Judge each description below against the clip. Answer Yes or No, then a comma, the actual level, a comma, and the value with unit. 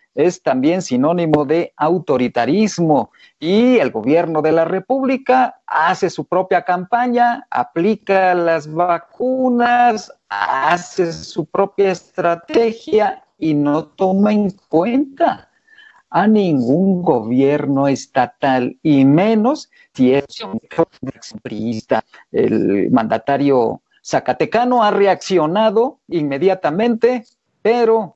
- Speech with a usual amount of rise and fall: No, wide, 7.2 semitones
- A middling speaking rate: No, slow, 90 wpm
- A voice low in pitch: No, medium, 185 Hz